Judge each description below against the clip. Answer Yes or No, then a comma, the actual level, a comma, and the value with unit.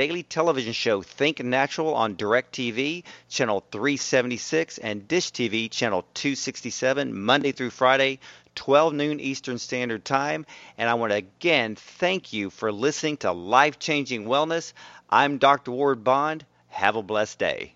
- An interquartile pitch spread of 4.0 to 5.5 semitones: Yes, average, 4.4 semitones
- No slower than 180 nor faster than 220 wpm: No, average, 140 wpm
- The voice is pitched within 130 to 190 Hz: Yes, low, 135 Hz